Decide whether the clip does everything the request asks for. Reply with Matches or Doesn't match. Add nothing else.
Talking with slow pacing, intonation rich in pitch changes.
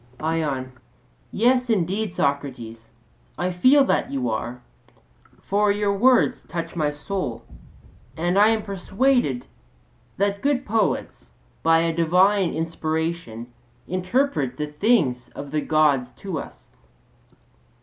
Matches